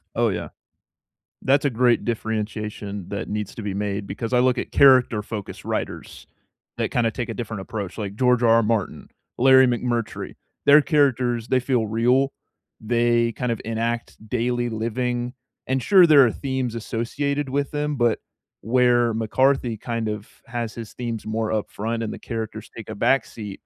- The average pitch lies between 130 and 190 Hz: No, low, 115 Hz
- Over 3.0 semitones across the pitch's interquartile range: No, narrow, 2.5 semitones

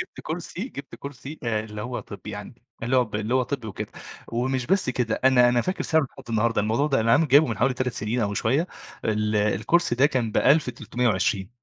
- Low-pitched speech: Yes, low, 120 Hz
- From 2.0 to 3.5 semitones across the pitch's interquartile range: No, average, 4.0 semitones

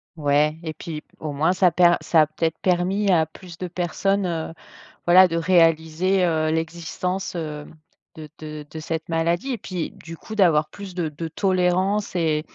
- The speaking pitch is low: No, medium, 165 Hz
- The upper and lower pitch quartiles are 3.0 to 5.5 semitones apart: No, narrow, 2.6 semitones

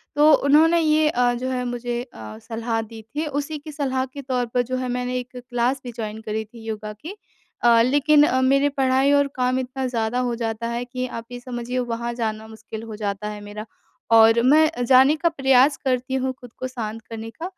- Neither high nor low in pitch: No, high, 245 Hz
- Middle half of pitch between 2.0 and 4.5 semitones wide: Yes, average, 3.0 semitones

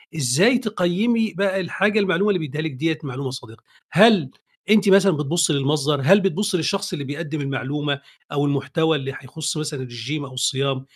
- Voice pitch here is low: No, medium, 155 Hz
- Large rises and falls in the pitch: Yes, wide, 5.8 semitones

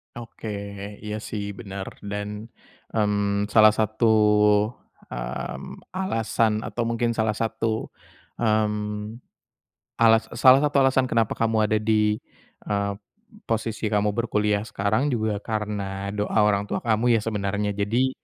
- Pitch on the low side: Yes, low, 110 Hz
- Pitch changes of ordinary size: No, narrow, 1.7 semitones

